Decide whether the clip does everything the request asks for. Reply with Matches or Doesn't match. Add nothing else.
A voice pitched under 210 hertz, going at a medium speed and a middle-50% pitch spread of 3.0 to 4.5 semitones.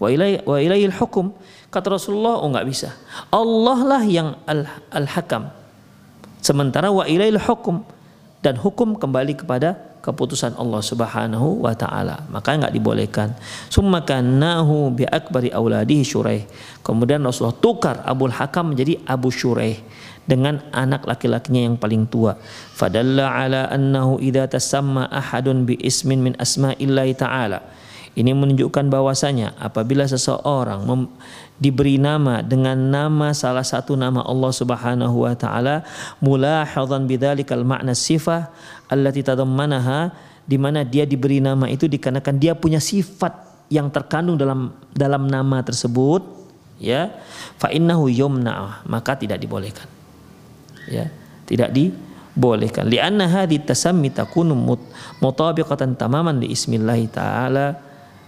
Matches